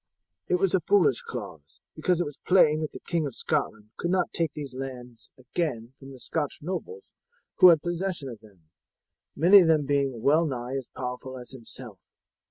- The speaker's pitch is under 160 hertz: Yes, medium, 140 Hz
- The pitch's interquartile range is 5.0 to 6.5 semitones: Yes, wide, 5.5 semitones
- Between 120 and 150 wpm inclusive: No, average, 185 wpm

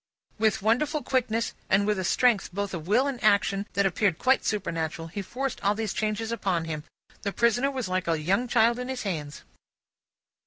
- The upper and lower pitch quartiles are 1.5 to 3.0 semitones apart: No, average, 4.3 semitones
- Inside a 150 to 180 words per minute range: No, average, 190 wpm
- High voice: Yes, high, 210 Hz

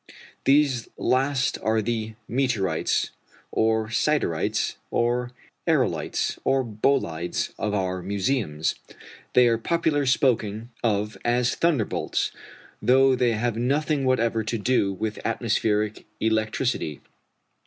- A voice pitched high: No, low, 115 Hz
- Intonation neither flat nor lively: Yes, average, 3.4 semitones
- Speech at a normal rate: No, slow, 105 wpm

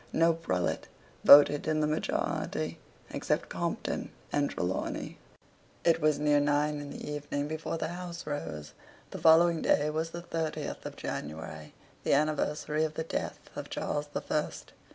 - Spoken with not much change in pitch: Yes, narrow, 1.8 semitones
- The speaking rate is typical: Yes, average, 155 wpm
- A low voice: No, medium, 150 Hz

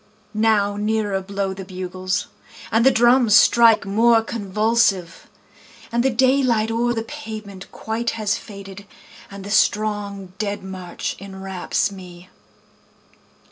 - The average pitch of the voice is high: Yes, high, 205 Hz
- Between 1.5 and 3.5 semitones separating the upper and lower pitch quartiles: Yes, average, 2.8 semitones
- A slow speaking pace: Yes, slow, 120 wpm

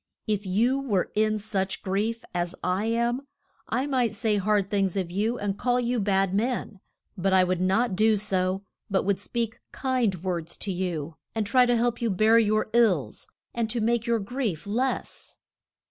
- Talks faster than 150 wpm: Yes, average, 180 wpm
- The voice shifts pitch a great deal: No, average, 3.6 semitones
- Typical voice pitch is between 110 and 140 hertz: No, high, 210 Hz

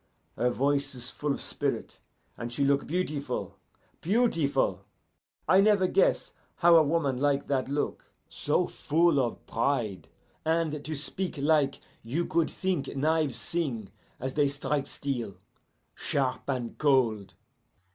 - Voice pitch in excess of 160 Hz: No, medium, 140 Hz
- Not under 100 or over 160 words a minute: Yes, slow, 135 wpm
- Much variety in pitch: No, average, 3.7 semitones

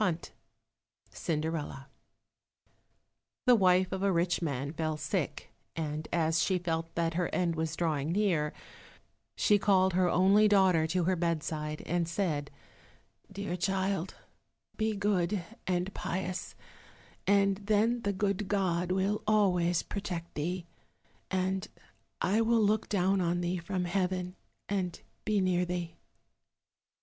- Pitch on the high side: No, medium, 180 Hz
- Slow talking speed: Yes, slow, 130 wpm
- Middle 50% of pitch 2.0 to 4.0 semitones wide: Yes, average, 2.9 semitones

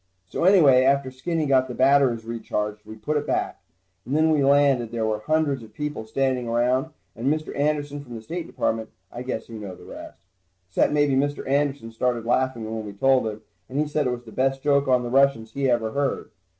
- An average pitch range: Yes, average, 3.8 semitones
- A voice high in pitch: No, low, 130 Hz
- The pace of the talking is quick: Yes, fast, 220 wpm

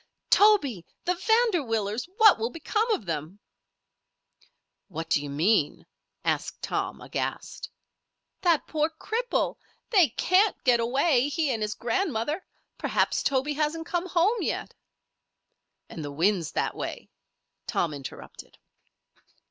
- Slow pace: Yes, slow, 115 wpm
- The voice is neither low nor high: No, very high, 280 Hz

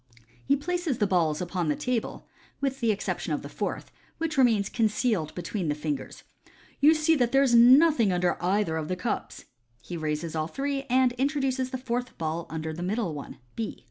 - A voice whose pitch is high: Yes, high, 220 Hz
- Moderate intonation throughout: No, wide, 7.9 semitones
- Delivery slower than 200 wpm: No, fast, 205 wpm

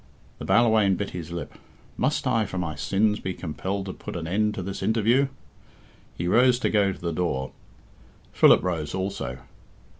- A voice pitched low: Yes, very low, 95 Hz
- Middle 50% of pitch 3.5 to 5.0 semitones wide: Yes, average, 4.0 semitones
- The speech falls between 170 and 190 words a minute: Yes, average, 175 wpm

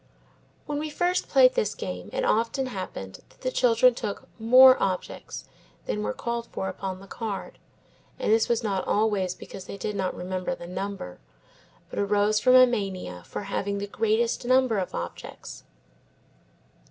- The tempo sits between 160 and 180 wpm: Yes, average, 165 wpm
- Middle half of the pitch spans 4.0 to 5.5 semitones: Yes, average, 4.7 semitones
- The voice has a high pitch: Yes, high, 210 Hz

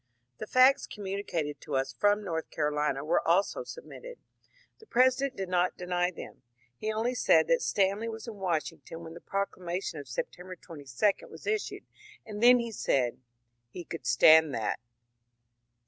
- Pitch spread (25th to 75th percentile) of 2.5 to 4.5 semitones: No, wide, 5.6 semitones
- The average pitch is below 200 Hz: Yes, medium, 185 Hz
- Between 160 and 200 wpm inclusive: Yes, average, 165 wpm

